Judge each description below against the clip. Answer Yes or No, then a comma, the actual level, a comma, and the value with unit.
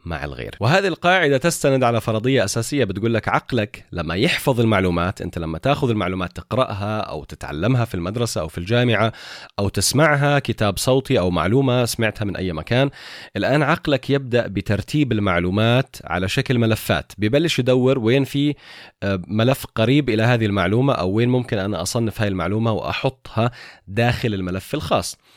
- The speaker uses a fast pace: Yes, fast, 150 wpm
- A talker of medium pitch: No, low, 115 Hz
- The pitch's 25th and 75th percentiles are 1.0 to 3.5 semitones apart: No, average, 5.1 semitones